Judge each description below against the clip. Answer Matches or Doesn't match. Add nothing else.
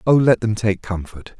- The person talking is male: Matches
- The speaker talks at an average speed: Doesn't match